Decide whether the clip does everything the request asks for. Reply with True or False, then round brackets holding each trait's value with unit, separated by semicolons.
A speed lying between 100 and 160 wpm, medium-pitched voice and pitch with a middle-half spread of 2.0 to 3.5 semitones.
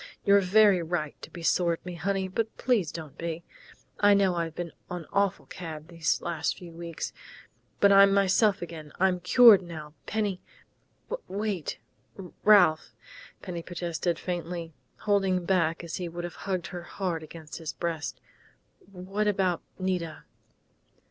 True (150 wpm; 180 Hz; 2.8 semitones)